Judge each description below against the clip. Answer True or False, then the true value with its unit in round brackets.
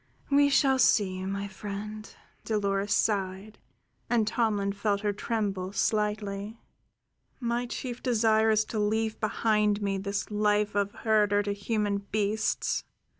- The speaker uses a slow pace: True (125 wpm)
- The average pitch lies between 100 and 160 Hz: False (210 Hz)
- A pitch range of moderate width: False (1.5 semitones)